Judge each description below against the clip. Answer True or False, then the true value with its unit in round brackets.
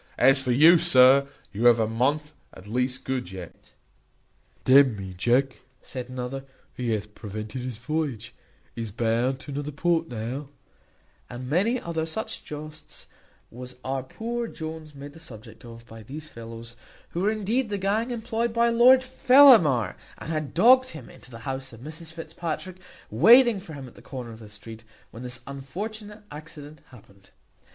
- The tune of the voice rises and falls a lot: True (6.2 semitones)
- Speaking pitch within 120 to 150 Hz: True (135 Hz)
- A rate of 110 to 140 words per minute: False (170 wpm)